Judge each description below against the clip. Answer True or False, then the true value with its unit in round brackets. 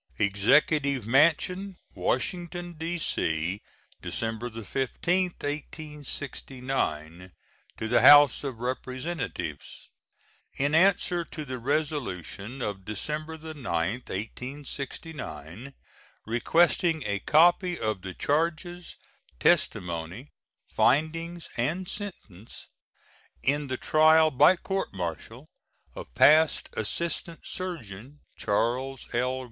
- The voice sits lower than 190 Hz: True (140 Hz)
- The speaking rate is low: True (85 wpm)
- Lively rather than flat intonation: True (6.4 semitones)